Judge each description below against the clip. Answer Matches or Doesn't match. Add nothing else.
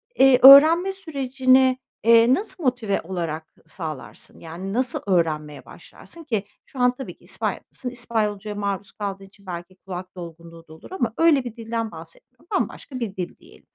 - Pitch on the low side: Doesn't match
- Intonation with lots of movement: Matches